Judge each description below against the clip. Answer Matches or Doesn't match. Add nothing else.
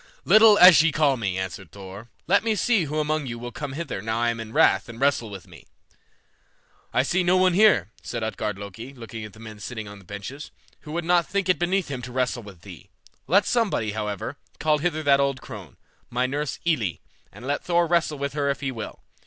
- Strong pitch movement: Matches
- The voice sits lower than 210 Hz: Matches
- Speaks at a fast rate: Matches